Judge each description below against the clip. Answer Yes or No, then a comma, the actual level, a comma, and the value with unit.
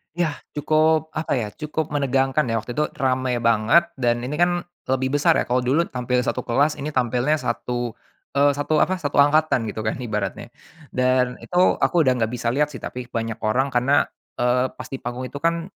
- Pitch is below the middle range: Yes, low, 130 Hz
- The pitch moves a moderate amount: Yes, average, 3.6 semitones